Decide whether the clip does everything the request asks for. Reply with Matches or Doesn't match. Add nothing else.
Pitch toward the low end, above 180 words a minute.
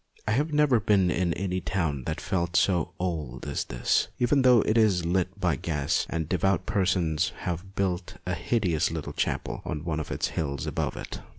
Matches